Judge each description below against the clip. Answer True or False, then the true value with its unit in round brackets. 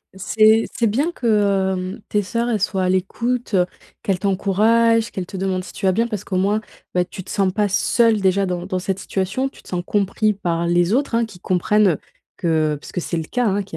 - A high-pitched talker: True (195 Hz)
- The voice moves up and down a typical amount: True (3.1 semitones)